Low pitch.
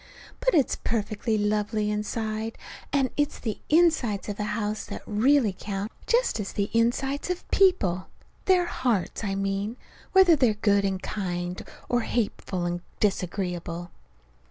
No: high, 215 Hz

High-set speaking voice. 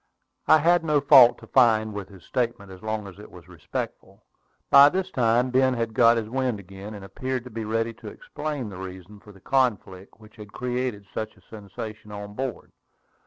No: low, 115 Hz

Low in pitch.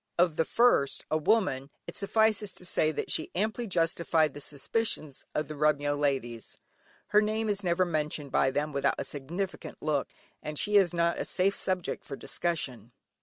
No: medium, 160 Hz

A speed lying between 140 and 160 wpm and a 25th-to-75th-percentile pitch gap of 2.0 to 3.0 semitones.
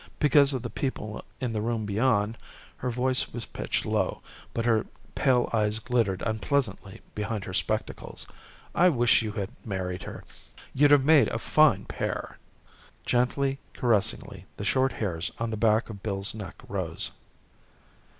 No: average, 150 wpm; average, 3.6 semitones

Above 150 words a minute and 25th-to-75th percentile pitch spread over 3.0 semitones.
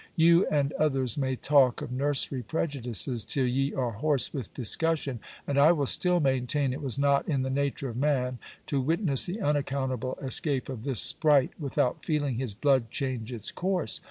No: average, 180 wpm; narrow, 2.5 semitones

